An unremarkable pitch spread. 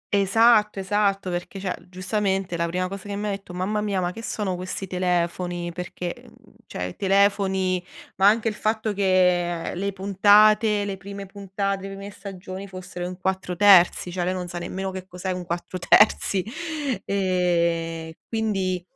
No: narrow, 1.9 semitones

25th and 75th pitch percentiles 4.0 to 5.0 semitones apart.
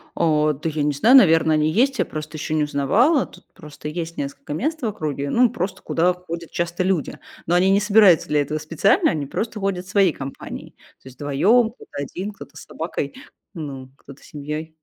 Yes: average, 4.7 semitones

